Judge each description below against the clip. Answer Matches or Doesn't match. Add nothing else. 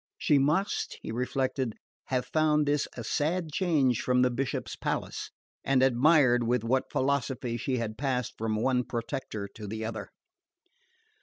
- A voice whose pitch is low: Matches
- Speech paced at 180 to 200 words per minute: Doesn't match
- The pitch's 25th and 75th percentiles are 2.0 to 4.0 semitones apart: Matches